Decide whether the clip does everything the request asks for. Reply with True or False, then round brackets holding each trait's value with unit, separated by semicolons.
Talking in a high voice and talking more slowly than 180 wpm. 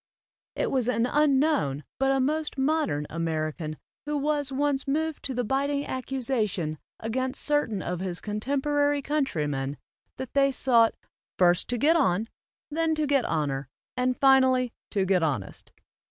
True (260 Hz; 145 wpm)